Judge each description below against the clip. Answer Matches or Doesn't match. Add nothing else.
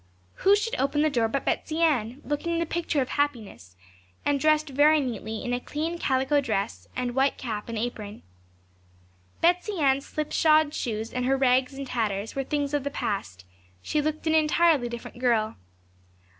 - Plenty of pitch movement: Doesn't match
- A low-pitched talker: Doesn't match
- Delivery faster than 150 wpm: Matches